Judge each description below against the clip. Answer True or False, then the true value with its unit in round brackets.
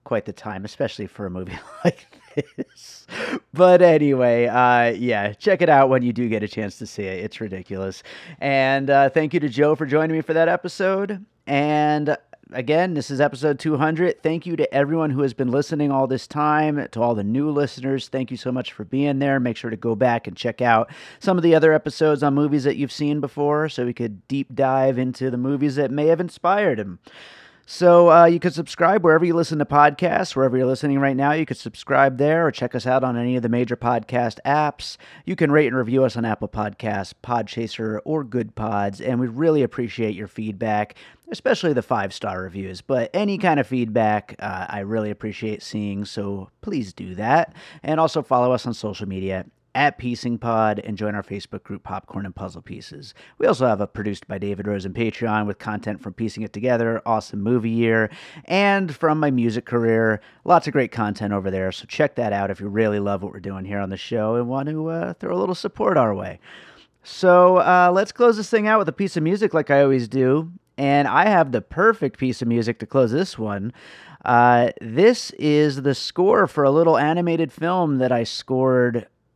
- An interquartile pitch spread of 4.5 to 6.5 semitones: True (5.5 semitones)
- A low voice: True (130 Hz)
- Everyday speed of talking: False (215 wpm)